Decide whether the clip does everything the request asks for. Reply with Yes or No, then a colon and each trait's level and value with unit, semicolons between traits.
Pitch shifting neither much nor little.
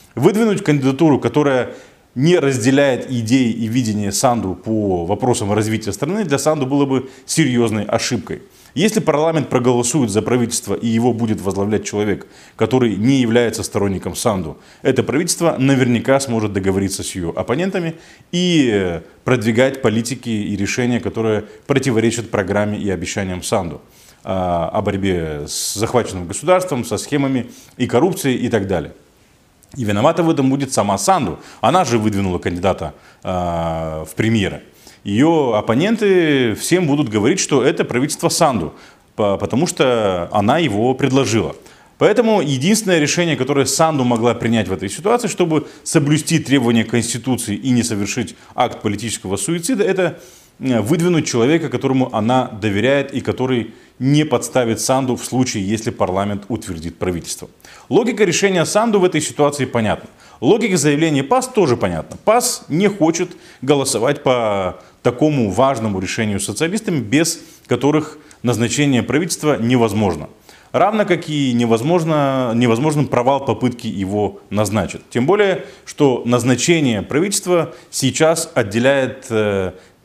No: wide, 6.0 semitones